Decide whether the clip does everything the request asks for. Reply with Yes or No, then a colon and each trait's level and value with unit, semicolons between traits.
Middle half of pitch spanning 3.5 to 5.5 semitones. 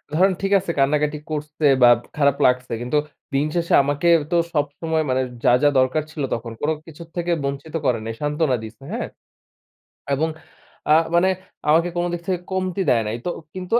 Yes: average, 3.9 semitones